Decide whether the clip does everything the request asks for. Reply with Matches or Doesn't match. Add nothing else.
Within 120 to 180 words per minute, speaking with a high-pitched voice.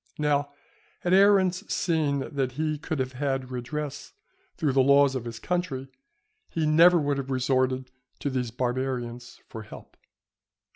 Doesn't match